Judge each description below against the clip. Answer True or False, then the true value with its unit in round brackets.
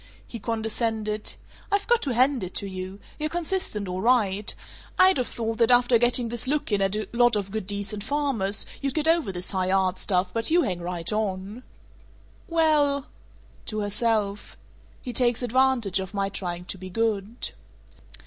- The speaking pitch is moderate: False (220 Hz)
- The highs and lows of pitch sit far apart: False (4.6 semitones)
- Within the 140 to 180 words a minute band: True (175 wpm)